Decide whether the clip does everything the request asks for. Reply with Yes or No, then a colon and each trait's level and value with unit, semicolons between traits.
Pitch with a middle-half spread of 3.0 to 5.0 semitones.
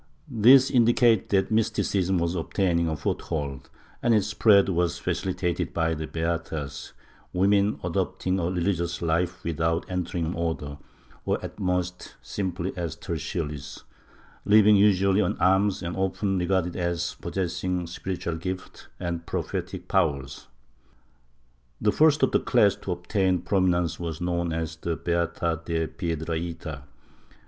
No: narrow, 2.6 semitones